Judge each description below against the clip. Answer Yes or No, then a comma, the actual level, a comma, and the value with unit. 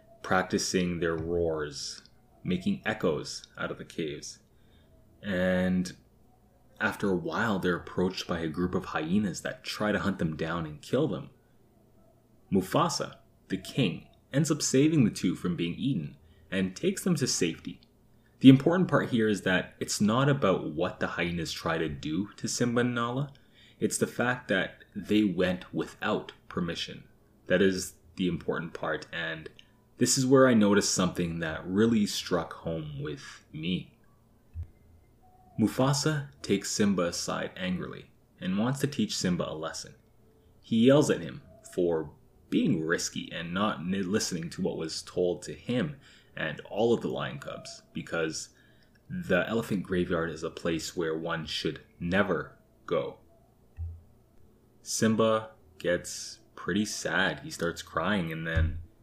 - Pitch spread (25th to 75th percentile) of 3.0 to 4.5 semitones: No, average, 5.2 semitones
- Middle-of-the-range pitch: No, low, 100 Hz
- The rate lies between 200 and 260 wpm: No, average, 150 wpm